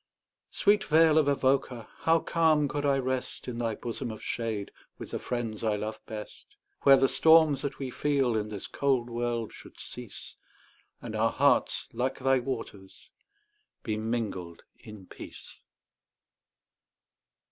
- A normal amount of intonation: Yes, average, 4.2 semitones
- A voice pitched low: Yes, low, 125 Hz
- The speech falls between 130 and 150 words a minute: Yes, average, 145 wpm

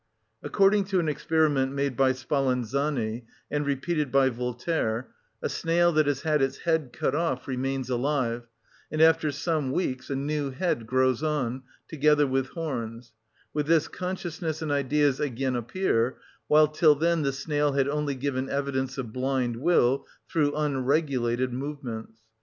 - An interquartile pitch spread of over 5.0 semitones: No, average, 3.0 semitones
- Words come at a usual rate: Yes, average, 150 wpm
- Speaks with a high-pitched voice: No, medium, 140 Hz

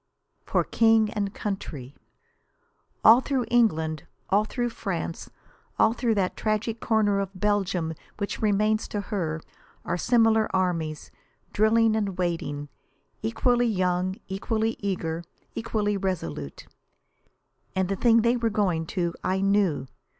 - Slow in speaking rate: Yes, slow, 125 wpm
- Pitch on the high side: Yes, high, 200 Hz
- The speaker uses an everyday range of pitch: Yes, average, 3.8 semitones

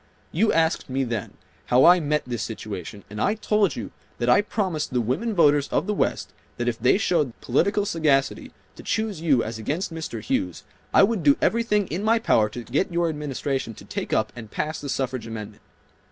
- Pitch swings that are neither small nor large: No, wide, 7.4 semitones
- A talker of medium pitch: Yes, medium, 145 Hz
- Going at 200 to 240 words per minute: Yes, fast, 205 wpm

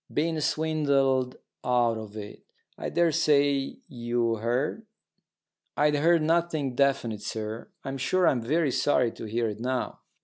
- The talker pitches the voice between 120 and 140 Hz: Yes, low, 135 Hz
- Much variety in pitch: No, average, 4.5 semitones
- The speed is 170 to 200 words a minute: No, slow, 135 wpm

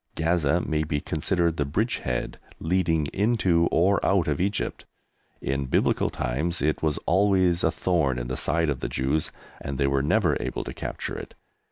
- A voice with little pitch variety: No, average, 4.1 semitones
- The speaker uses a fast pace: No, average, 175 wpm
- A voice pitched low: Yes, very low, 80 Hz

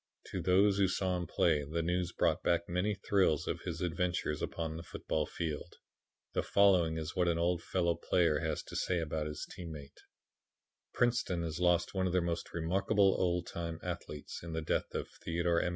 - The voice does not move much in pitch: Yes, narrow, 1.9 semitones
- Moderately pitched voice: No, very low, 85 Hz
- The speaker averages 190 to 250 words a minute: Yes, average, 195 wpm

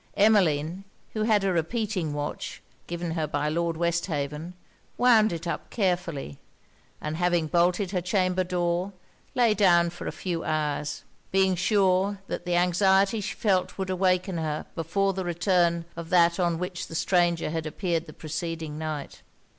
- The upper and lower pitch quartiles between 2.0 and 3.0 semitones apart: Yes, average, 2.7 semitones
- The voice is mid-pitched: Yes, medium, 175 Hz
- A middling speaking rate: Yes, average, 155 wpm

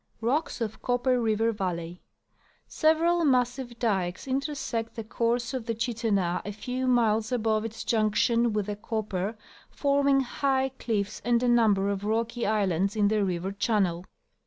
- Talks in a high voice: Yes, high, 225 Hz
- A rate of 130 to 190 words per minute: Yes, average, 155 wpm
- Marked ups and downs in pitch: No, average, 3.3 semitones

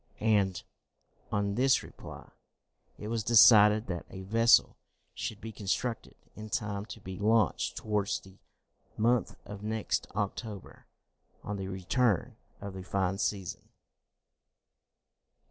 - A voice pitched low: Yes, low, 105 Hz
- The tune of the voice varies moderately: No, narrow, 2.3 semitones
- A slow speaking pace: Yes, slow, 120 wpm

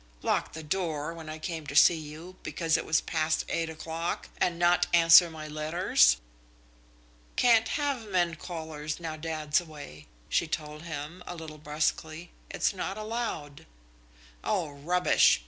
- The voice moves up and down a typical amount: No, narrow, 2.3 semitones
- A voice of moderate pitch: Yes, medium, 160 Hz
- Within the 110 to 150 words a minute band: Yes, average, 145 wpm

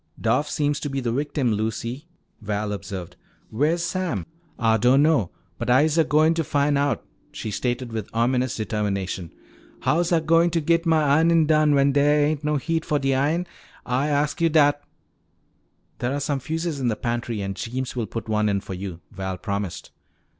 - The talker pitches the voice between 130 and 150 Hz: Yes, medium, 140 Hz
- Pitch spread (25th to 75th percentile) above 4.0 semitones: Yes, wide, 5.6 semitones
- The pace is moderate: Yes, average, 190 wpm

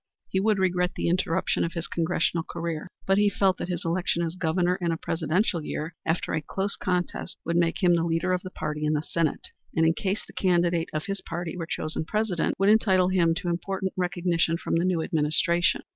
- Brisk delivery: Yes, fast, 215 wpm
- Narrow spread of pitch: Yes, narrow, 2.0 semitones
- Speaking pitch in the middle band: Yes, medium, 175 Hz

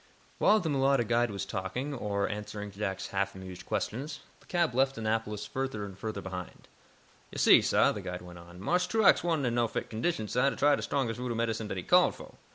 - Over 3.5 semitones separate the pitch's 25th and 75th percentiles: Yes, average, 5.2 semitones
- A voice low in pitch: Yes, low, 115 Hz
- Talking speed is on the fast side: Yes, fast, 215 wpm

